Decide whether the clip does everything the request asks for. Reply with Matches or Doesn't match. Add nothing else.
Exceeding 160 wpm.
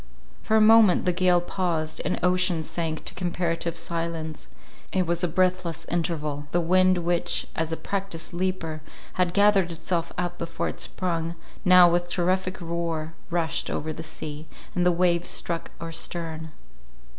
Doesn't match